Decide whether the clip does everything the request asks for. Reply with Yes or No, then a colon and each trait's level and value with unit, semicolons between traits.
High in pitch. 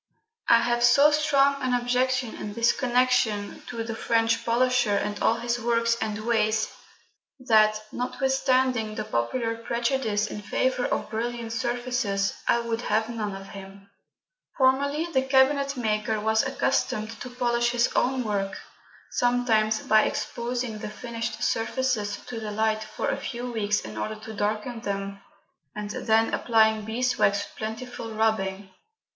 Yes: high, 230 Hz